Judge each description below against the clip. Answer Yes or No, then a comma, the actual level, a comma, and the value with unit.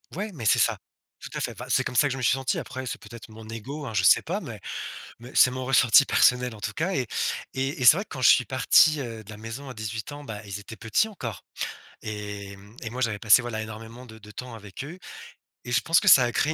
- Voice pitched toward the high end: No, low, 120 Hz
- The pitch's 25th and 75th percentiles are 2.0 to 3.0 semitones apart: No, average, 3.4 semitones